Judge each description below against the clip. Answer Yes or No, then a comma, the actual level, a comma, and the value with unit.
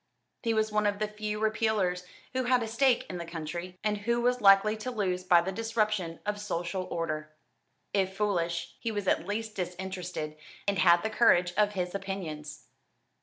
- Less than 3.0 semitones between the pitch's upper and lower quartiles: No, average, 3.3 semitones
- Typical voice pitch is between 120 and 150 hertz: No, high, 195 Hz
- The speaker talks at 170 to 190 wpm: Yes, average, 180 wpm